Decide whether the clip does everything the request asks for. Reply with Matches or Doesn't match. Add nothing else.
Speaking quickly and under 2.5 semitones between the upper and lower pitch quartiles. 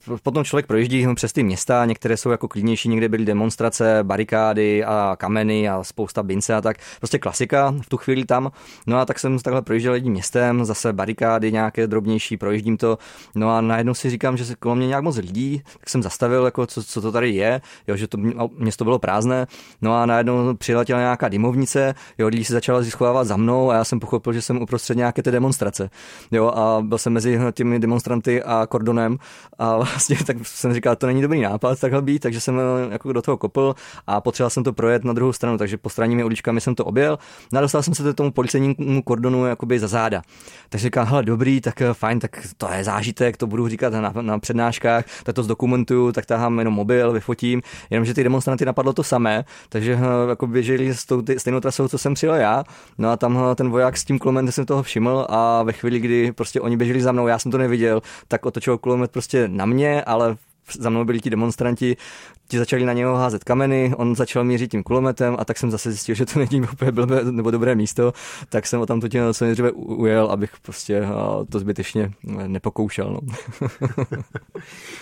Matches